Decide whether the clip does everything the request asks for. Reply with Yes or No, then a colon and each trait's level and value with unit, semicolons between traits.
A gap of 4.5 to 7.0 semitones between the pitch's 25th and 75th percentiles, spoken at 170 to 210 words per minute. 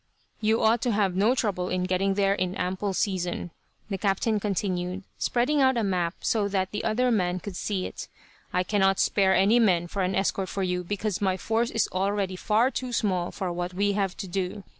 No: narrow, 2.6 semitones; fast, 205 wpm